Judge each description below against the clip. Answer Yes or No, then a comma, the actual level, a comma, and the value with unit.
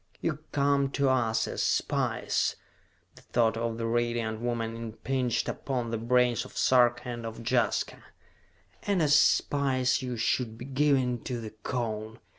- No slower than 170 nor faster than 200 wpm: No, average, 150 wpm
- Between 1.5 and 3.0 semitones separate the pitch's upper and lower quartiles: Yes, narrow, 2.4 semitones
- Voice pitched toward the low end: Yes, low, 120 Hz